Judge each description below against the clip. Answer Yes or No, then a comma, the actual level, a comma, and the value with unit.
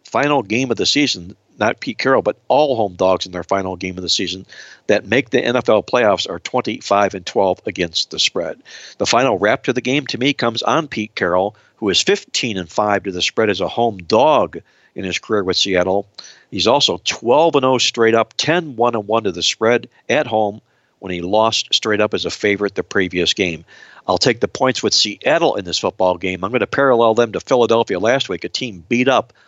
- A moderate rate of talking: No, fast, 220 wpm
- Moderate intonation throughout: Yes, average, 4.2 semitones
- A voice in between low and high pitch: No, low, 105 Hz